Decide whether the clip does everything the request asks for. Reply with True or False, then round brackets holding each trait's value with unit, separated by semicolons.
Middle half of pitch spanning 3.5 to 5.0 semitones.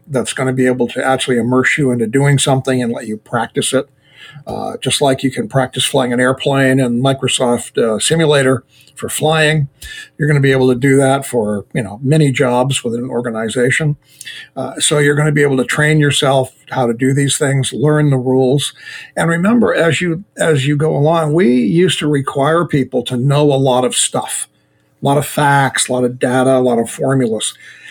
False (2.7 semitones)